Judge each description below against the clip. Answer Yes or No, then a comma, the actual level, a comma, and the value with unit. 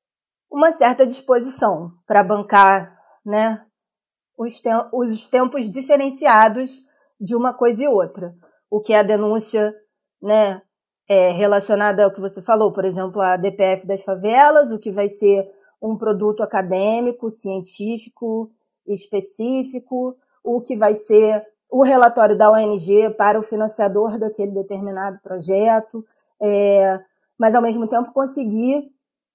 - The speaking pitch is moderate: No, high, 215 Hz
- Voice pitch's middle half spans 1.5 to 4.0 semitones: Yes, average, 3.0 semitones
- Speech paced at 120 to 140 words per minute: Yes, average, 130 wpm